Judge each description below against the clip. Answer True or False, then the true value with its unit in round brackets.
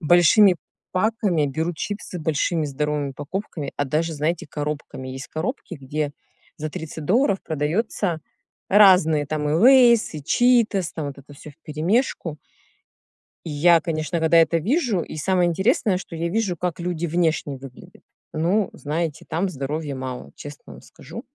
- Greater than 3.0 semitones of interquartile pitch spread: True (3.9 semitones)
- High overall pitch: False (165 Hz)